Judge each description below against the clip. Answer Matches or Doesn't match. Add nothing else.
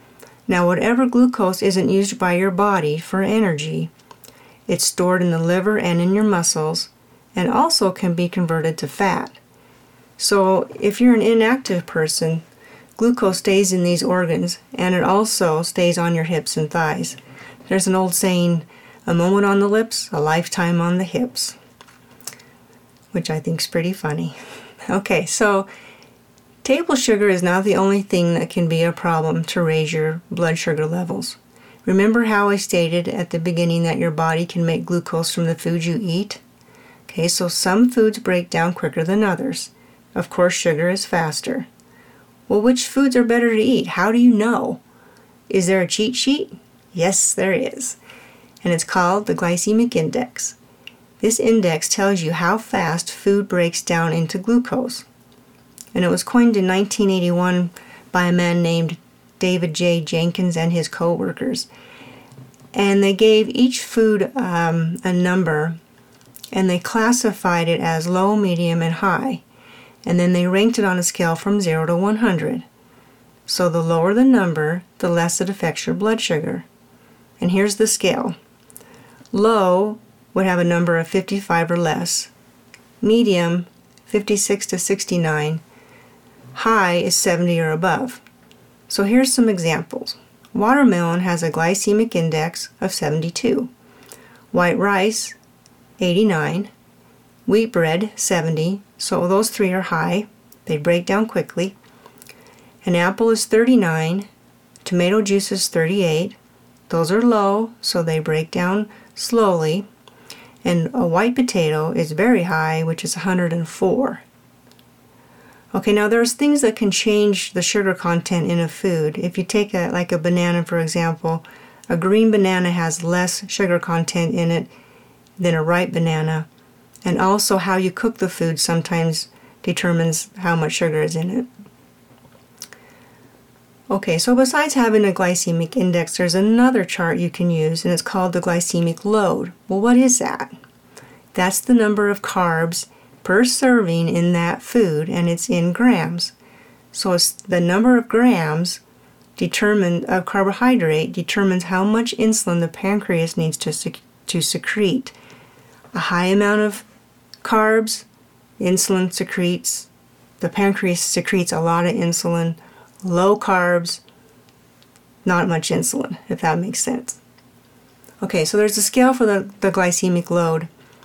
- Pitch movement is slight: Doesn't match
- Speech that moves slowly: Doesn't match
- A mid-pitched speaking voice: Matches